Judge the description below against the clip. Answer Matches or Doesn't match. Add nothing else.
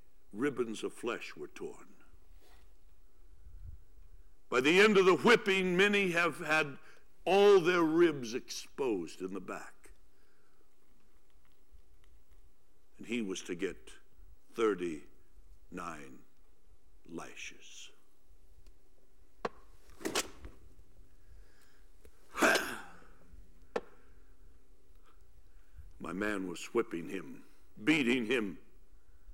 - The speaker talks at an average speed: Doesn't match